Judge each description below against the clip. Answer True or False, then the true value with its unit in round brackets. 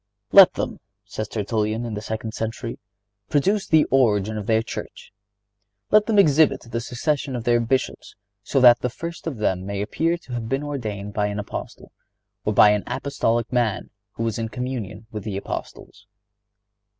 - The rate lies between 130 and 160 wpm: False (175 wpm)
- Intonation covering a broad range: False (4.2 semitones)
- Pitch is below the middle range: True (115 Hz)